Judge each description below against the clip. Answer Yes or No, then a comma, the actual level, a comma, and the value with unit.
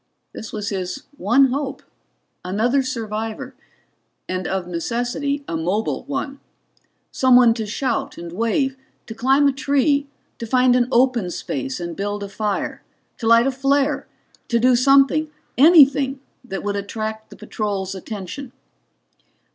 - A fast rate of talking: No, average, 140 wpm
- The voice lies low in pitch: No, high, 235 Hz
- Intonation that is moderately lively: Yes, average, 4.9 semitones